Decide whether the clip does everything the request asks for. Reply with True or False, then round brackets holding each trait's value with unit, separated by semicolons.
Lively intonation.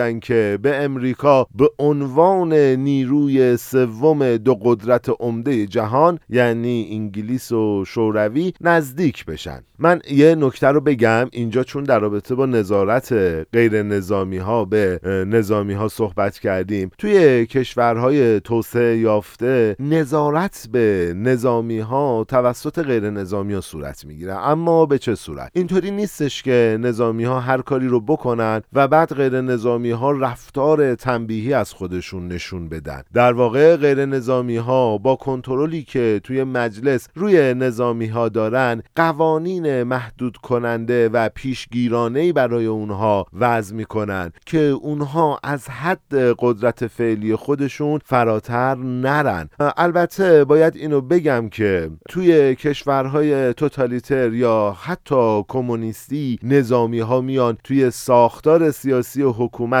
False (4.0 semitones)